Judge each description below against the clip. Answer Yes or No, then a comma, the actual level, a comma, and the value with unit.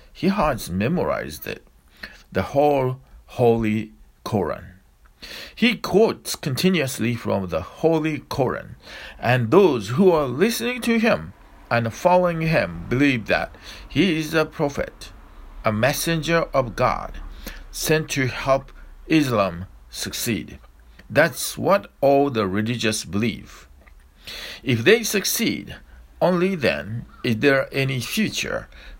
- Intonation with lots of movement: Yes, wide, 8.4 semitones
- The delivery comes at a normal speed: No, slow, 115 wpm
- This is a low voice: Yes, low, 130 Hz